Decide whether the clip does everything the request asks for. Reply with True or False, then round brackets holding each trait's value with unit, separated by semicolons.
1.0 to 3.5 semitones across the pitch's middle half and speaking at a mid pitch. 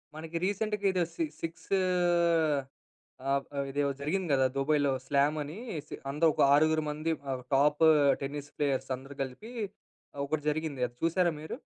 True (2.9 semitones; 150 Hz)